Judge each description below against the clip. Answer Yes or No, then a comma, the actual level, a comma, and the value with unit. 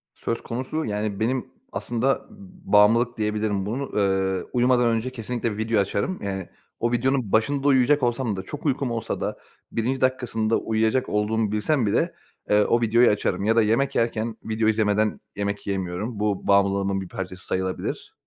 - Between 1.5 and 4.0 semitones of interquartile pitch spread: Yes, average, 3.2 semitones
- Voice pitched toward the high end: No, low, 110 Hz